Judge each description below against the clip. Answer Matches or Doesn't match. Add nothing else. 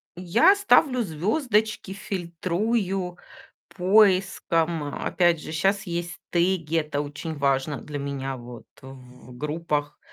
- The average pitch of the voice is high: Doesn't match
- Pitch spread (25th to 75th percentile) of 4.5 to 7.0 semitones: Matches